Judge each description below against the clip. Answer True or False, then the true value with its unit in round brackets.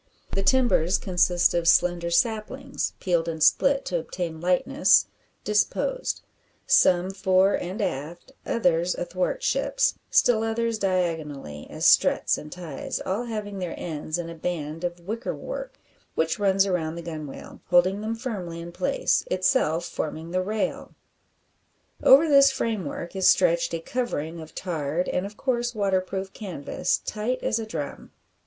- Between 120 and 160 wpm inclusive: True (145 wpm)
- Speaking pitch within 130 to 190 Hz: True (185 Hz)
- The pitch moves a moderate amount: True (4.5 semitones)